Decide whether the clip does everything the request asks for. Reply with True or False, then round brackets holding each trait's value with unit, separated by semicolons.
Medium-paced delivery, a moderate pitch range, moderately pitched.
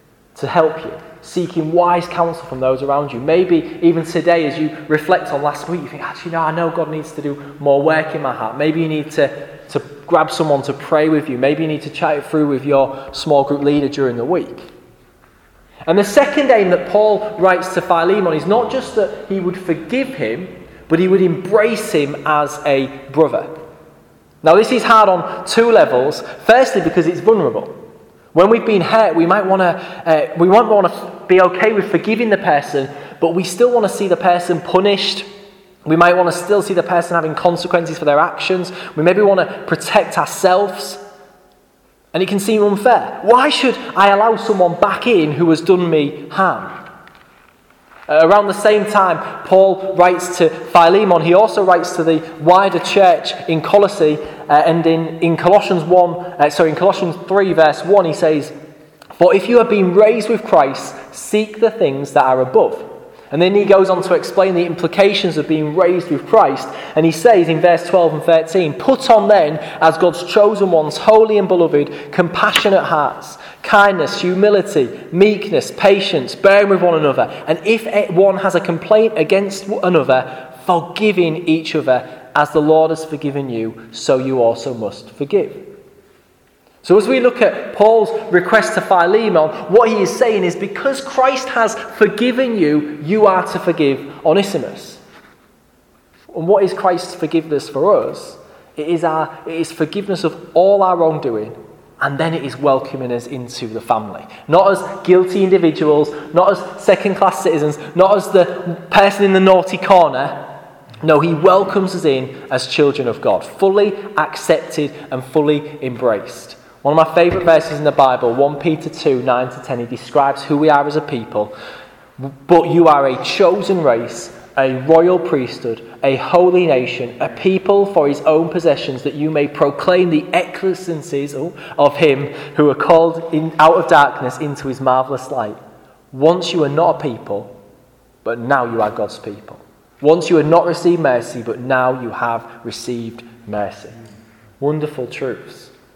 True (180 wpm; 4.7 semitones; 170 Hz)